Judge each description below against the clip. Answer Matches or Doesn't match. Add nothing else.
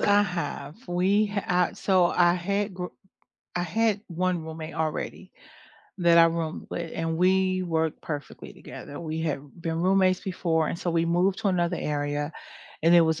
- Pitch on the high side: Doesn't match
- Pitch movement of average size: Doesn't match